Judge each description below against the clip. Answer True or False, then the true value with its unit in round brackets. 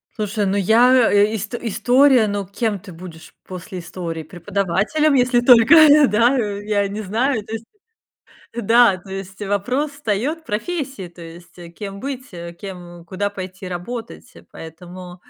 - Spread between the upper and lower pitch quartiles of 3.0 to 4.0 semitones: False (4.8 semitones)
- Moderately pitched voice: False (205 Hz)